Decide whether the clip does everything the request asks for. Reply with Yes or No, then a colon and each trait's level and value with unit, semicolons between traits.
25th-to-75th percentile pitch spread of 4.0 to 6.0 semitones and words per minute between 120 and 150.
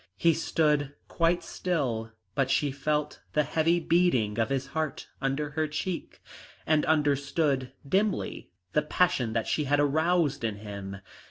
No: average, 3.4 semitones; average, 145 wpm